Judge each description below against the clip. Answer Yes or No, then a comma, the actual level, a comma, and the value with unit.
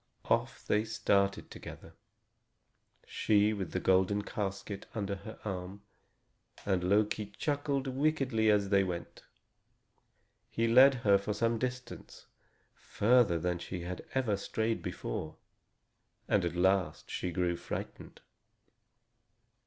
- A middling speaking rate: No, slow, 115 wpm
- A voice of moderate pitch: No, low, 100 Hz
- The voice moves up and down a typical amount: Yes, average, 3.3 semitones